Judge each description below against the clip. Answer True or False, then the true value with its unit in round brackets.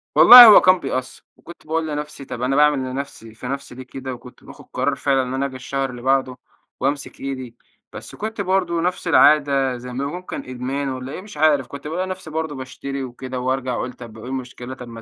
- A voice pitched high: False (135 Hz)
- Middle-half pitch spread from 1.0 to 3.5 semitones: True (3.1 semitones)